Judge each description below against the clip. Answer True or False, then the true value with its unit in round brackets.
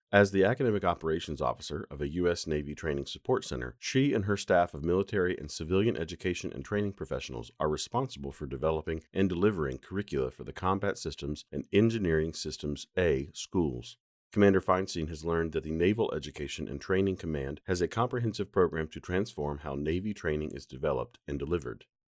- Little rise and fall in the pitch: False (4.6 semitones)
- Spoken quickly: False (175 wpm)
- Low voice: True (85 Hz)